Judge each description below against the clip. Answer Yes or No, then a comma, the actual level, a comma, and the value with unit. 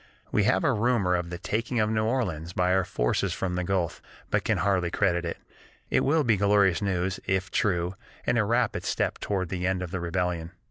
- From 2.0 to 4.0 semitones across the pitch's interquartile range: Yes, average, 3.0 semitones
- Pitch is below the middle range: Yes, very low, 95 Hz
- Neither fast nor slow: No, fast, 215 wpm